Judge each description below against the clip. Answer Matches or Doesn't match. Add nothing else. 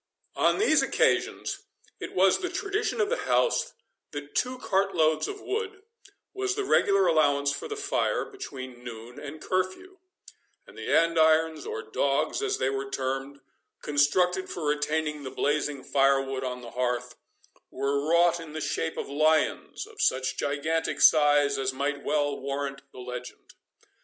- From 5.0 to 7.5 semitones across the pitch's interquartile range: Matches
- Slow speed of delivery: Doesn't match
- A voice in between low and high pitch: Matches